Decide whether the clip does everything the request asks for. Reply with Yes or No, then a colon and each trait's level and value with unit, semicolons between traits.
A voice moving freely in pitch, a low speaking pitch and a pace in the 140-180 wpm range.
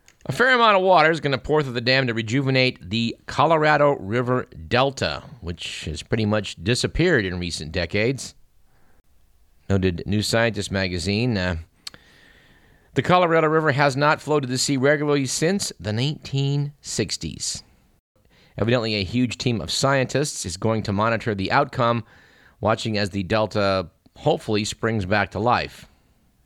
Yes: wide, 5.8 semitones; low, 115 Hz; average, 145 wpm